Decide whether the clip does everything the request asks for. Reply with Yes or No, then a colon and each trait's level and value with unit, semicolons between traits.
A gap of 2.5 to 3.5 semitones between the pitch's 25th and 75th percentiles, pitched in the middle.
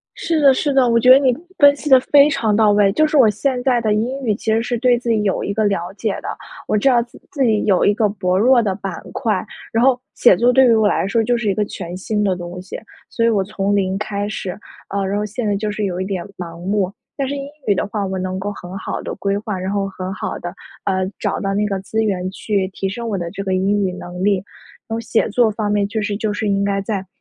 No: average, 3.1 semitones; high, 210 Hz